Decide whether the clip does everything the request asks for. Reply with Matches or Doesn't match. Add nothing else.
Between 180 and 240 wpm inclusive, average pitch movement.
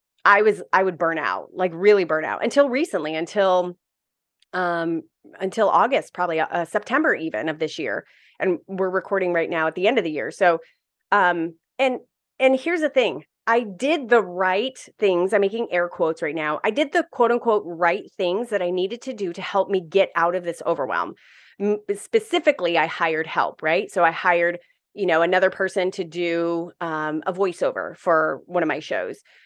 Matches